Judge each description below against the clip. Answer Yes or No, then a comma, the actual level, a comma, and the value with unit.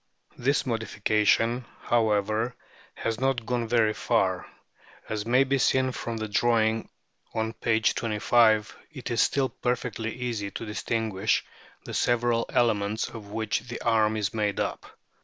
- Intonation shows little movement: Yes, narrow, 1.9 semitones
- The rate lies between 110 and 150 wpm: Yes, average, 140 wpm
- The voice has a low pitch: Yes, low, 115 Hz